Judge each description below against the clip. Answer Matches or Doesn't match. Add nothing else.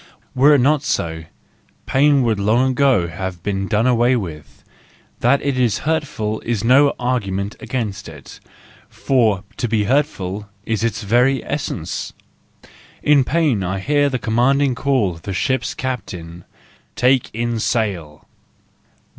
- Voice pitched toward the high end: Doesn't match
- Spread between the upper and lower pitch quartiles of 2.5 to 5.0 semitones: Doesn't match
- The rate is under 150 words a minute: Matches